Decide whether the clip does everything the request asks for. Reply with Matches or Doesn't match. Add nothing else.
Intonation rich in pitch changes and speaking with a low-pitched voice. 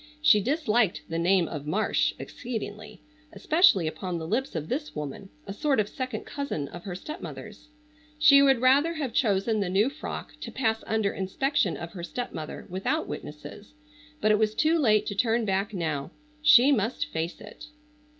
Doesn't match